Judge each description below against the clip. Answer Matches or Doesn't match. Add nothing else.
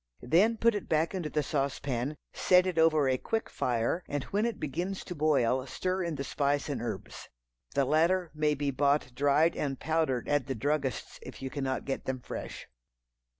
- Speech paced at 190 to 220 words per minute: Matches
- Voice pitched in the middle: Matches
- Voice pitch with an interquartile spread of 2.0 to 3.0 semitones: Doesn't match